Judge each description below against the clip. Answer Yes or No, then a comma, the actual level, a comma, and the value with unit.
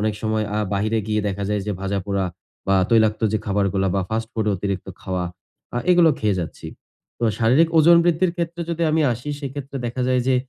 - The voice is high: No, low, 110 Hz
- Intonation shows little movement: No, wide, 5.8 semitones